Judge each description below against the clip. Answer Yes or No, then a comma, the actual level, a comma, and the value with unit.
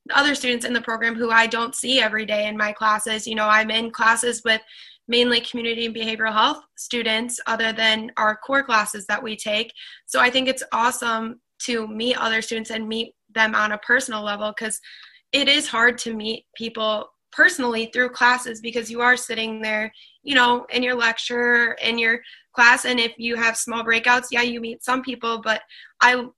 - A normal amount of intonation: No, narrow, 1.6 semitones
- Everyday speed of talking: Yes, average, 195 wpm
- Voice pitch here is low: No, high, 230 Hz